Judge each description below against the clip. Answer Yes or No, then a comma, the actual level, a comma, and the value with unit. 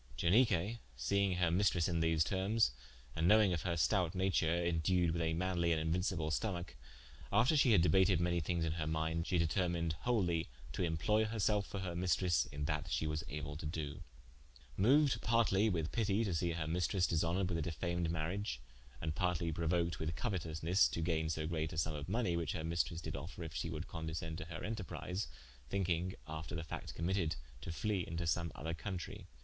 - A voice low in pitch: Yes, very low, 85 Hz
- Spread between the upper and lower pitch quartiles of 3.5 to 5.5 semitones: No, average, 2.8 semitones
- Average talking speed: Yes, average, 190 wpm